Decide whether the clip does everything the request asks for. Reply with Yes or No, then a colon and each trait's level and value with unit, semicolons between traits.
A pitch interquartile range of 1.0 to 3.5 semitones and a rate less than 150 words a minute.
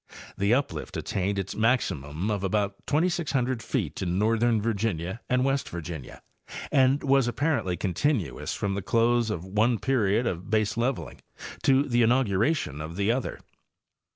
No: average, 4.9 semitones; average, 140 wpm